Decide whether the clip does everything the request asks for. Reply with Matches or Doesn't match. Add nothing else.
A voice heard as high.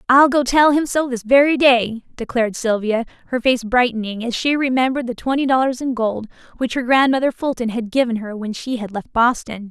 Matches